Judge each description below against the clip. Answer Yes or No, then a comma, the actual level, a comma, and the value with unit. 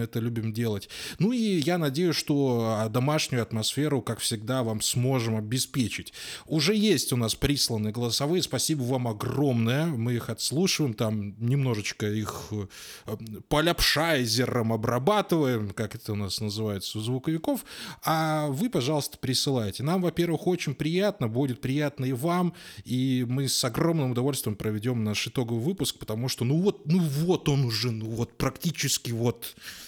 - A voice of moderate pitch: No, low, 130 Hz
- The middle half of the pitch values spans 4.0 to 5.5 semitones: Yes, average, 5.1 semitones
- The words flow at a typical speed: Yes, average, 145 wpm